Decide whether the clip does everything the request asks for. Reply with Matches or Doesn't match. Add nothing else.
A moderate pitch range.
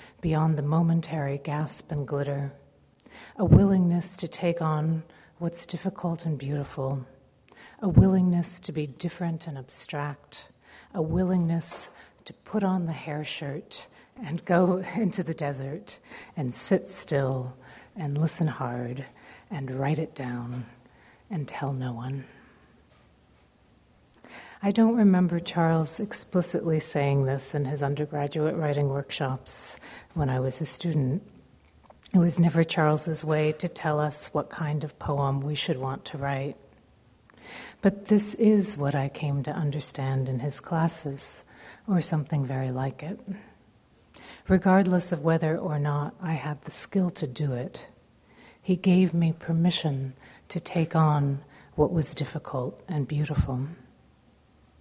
Matches